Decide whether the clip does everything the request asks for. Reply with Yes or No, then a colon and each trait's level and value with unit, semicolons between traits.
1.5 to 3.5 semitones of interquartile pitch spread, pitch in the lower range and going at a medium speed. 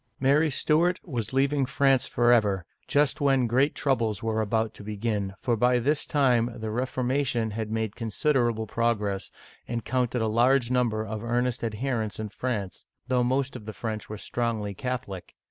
Yes: average, 3.0 semitones; low, 120 Hz; average, 165 wpm